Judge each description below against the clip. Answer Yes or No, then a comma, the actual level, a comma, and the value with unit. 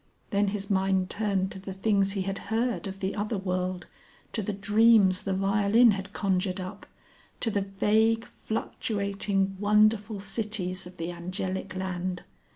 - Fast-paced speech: No, average, 155 wpm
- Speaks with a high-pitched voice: Yes, high, 195 Hz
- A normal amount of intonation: No, narrow, 1.9 semitones